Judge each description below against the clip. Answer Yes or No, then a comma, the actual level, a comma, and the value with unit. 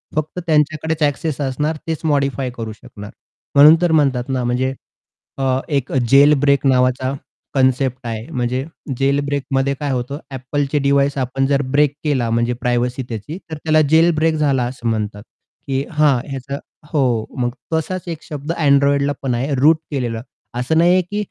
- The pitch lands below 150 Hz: Yes, medium, 140 Hz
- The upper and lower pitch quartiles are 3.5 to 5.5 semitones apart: No, average, 2.9 semitones